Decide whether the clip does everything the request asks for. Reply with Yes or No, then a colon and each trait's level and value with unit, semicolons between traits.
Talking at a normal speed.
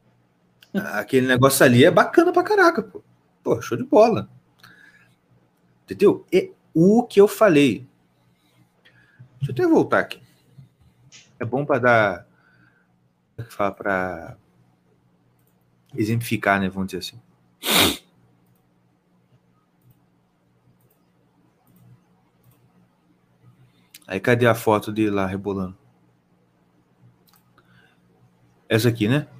No: slow, 90 wpm